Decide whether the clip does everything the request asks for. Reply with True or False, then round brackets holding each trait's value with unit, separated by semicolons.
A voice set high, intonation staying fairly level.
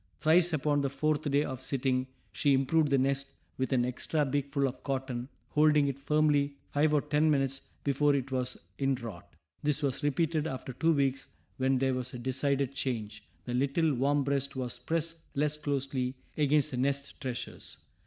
False (140 Hz; 2.1 semitones)